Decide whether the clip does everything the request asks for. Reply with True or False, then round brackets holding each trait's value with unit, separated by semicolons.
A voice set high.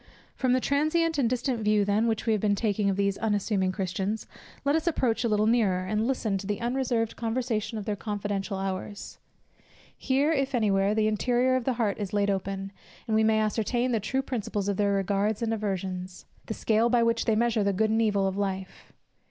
True (215 Hz)